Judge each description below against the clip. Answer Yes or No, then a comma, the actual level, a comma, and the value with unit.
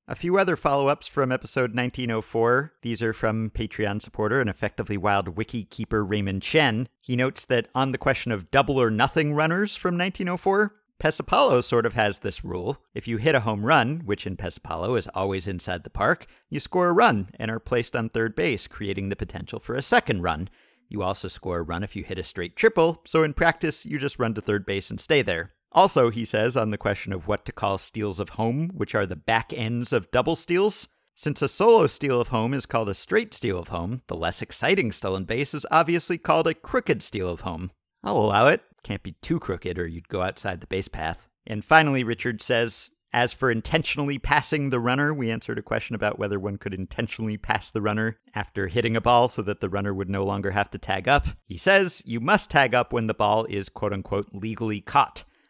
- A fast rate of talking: Yes, fast, 220 wpm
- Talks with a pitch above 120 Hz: No, low, 115 Hz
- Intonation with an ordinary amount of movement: No, wide, 5.7 semitones